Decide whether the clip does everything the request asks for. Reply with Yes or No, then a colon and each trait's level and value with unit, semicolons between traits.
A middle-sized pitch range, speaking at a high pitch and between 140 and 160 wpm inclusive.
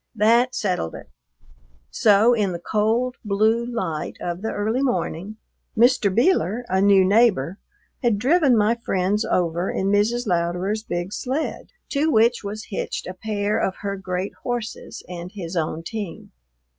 Yes: average, 4.0 semitones; high, 205 Hz; average, 150 wpm